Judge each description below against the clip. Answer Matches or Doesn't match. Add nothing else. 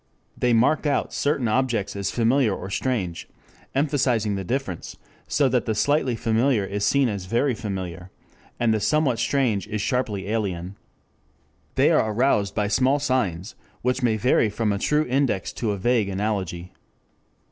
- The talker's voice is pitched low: Matches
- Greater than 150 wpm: Matches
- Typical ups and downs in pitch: Matches